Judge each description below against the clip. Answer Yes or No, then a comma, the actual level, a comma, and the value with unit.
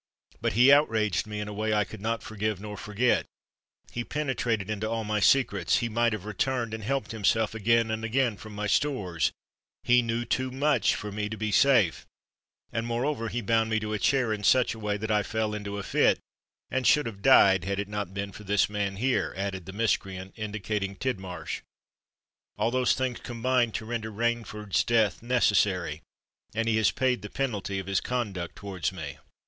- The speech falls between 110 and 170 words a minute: No, average, 185 wpm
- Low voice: Yes, low, 110 Hz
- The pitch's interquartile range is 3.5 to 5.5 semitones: No, average, 2.7 semitones